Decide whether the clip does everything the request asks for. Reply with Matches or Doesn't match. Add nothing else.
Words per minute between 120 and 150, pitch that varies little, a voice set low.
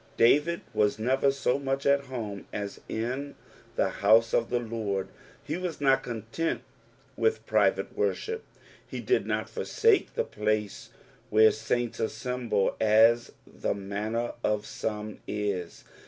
Doesn't match